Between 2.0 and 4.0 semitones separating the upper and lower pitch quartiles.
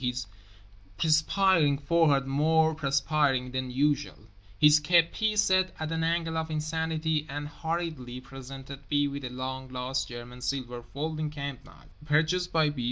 Yes: average, 3.4 semitones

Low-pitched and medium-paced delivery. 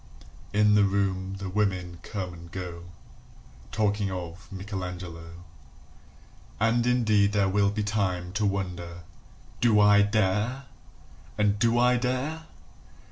No: low, 100 Hz; slow, 120 wpm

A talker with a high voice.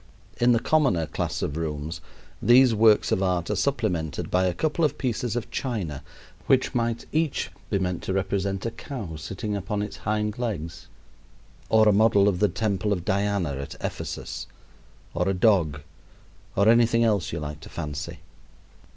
No: low, 100 Hz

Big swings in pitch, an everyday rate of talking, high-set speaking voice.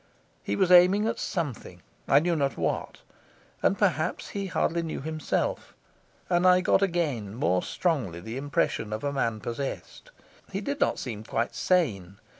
No: wide, 8.2 semitones; average, 160 wpm; medium, 145 Hz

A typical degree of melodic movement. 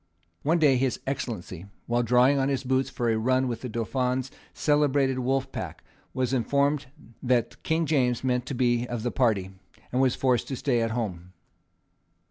No: narrow, 2.1 semitones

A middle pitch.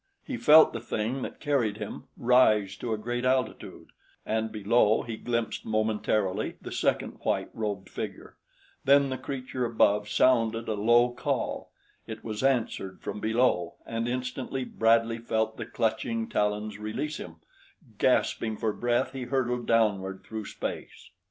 No: low, 115 Hz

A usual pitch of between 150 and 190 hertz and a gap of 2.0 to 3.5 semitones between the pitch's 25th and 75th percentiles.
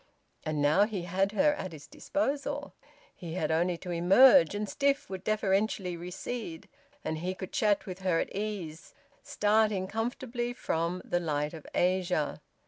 No: medium, 185 Hz; average, 4.1 semitones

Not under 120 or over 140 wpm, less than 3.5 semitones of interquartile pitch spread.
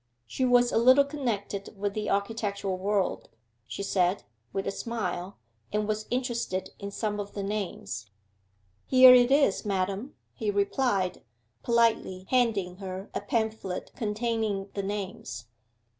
Yes: slow, 135 wpm; average, 3.1 semitones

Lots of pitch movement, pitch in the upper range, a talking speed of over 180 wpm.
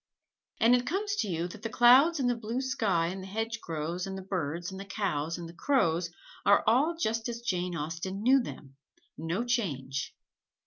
Yes: wide, 6.1 semitones; high, 195 Hz; average, 190 wpm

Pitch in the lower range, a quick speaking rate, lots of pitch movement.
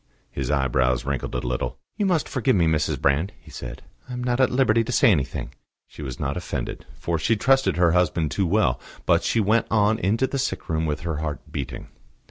Yes: very low, 85 Hz; fast, 215 wpm; wide, 8.4 semitones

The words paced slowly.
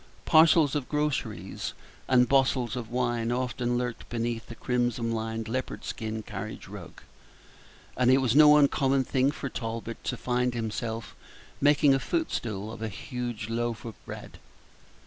No: average, 145 wpm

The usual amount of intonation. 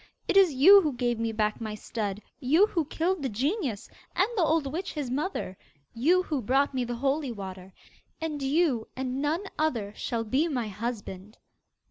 No: wide, 5.8 semitones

